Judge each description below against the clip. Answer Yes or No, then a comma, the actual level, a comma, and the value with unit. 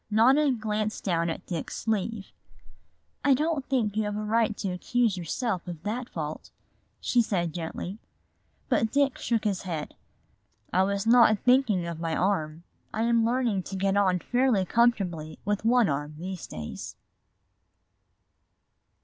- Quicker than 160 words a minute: No, average, 150 wpm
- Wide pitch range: No, average, 4.7 semitones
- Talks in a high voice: Yes, high, 205 Hz